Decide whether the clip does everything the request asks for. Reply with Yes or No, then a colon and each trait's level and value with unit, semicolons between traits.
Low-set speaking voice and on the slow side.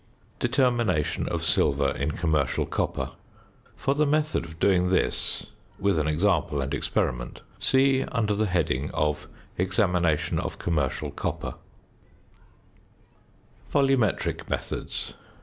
Yes: very low, 90 Hz; slow, 110 wpm